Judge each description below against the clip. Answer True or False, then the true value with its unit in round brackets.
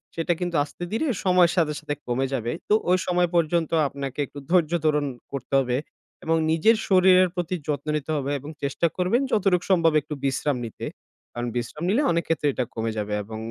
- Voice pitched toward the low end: False (160 Hz)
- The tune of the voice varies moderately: True (4.6 semitones)